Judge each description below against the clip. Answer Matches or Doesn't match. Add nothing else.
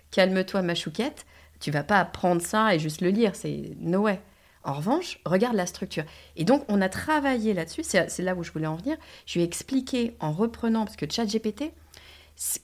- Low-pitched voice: Doesn't match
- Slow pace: Doesn't match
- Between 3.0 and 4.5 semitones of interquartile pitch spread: Doesn't match